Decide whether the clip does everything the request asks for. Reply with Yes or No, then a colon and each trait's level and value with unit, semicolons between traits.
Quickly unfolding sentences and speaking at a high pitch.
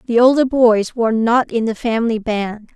No: average, 195 wpm; high, 230 Hz